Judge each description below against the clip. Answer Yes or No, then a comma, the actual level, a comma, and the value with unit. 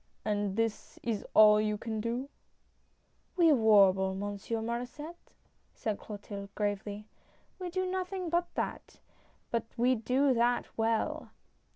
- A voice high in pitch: Yes, high, 225 Hz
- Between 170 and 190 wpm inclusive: No, slow, 135 wpm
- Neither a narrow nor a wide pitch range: Yes, average, 3.8 semitones